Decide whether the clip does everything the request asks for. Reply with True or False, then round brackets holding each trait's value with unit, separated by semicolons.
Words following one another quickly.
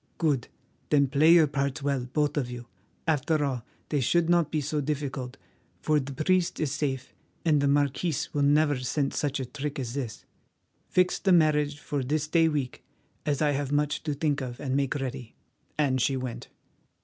False (185 wpm)